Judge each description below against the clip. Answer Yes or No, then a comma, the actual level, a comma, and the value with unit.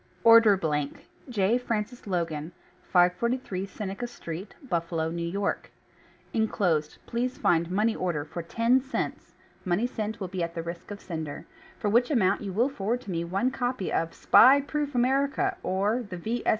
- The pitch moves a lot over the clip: Yes, wide, 5.9 semitones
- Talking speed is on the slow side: No, average, 165 wpm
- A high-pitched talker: Yes, high, 200 Hz